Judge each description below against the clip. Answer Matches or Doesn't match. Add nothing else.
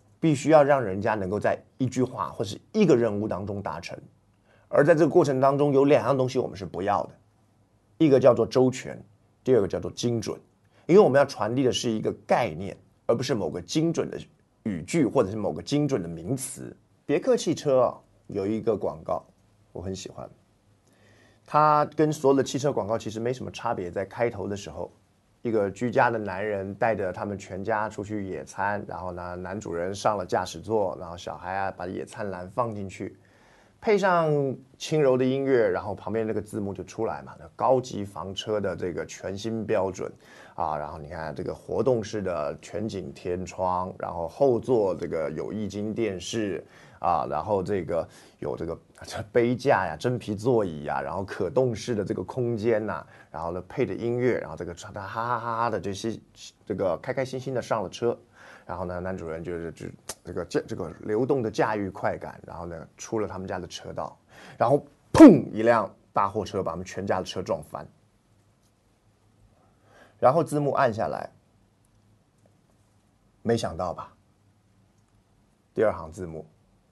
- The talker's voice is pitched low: Matches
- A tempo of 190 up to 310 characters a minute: Matches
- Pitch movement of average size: Matches